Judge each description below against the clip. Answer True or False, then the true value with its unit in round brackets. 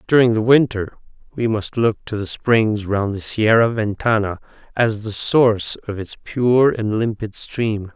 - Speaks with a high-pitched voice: False (110 Hz)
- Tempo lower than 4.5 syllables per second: True (4.2 syllables/s)